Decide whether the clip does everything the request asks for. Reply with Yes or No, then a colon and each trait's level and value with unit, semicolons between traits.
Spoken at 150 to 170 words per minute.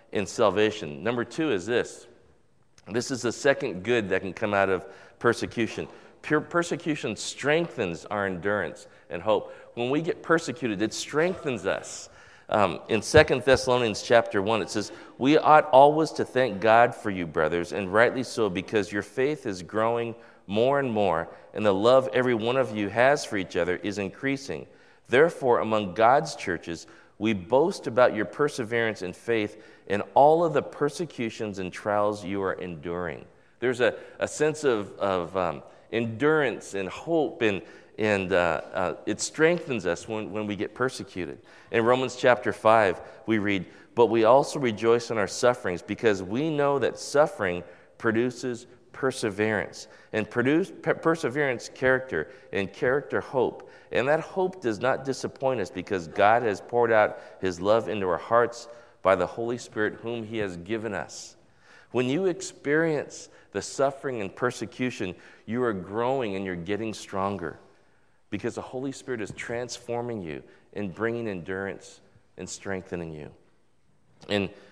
Yes: average, 160 wpm